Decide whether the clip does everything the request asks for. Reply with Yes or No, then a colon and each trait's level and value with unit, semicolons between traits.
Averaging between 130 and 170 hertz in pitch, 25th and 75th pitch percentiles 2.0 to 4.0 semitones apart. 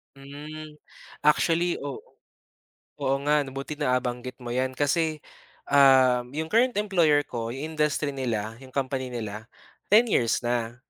Yes: medium, 140 Hz; average, 3.4 semitones